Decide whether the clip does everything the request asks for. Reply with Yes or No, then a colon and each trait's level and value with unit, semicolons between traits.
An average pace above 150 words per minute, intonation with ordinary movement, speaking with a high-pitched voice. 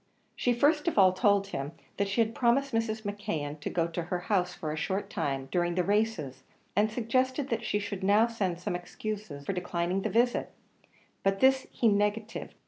Yes: average, 195 wpm; average, 4.2 semitones; high, 205 Hz